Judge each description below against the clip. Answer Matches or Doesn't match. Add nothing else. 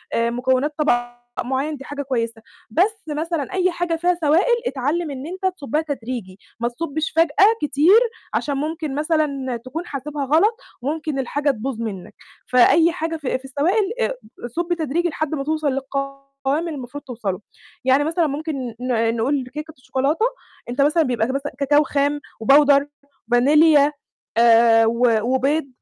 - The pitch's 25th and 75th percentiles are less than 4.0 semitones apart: Matches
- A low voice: Doesn't match